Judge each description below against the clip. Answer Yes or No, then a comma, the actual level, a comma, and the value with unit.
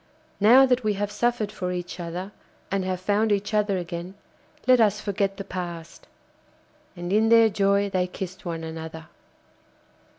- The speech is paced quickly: No, average, 160 wpm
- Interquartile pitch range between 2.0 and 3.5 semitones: Yes, average, 2.8 semitones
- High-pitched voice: Yes, high, 195 Hz